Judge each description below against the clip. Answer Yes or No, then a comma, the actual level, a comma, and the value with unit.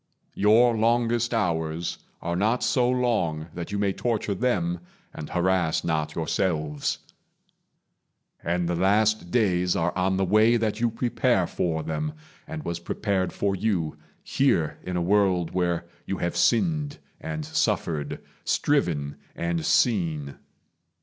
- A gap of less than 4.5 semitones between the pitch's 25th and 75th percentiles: No, average, 5.2 semitones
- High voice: No, very low, 95 Hz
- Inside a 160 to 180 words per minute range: No, slow, 135 wpm